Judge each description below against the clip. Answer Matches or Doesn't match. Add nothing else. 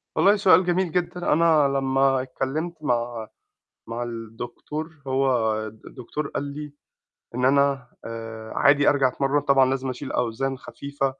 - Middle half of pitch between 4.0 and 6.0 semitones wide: Doesn't match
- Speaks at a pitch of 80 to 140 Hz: Matches